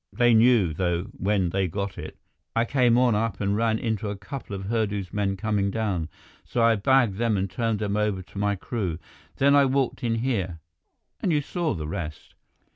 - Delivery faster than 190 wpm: Yes, average, 200 wpm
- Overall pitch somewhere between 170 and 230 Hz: No, low, 105 Hz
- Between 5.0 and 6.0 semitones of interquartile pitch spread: No, average, 3.4 semitones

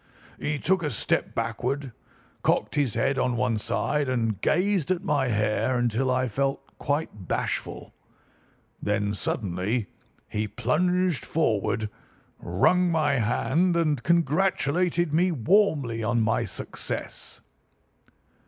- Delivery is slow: Yes, slow, 115 wpm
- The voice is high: No, low, 135 Hz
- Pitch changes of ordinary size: No, wide, 6.5 semitones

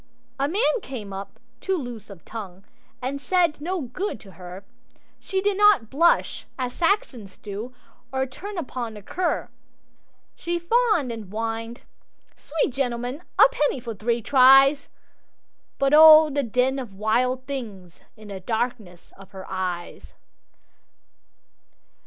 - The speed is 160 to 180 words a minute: No, slow, 135 wpm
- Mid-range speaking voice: No, very high, 250 Hz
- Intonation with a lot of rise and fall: Yes, wide, 5.8 semitones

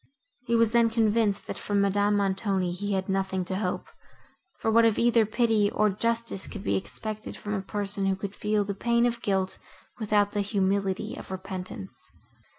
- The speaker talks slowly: No, average, 180 wpm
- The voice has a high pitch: Yes, high, 205 Hz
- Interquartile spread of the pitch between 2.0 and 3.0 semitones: Yes, narrow, 2.4 semitones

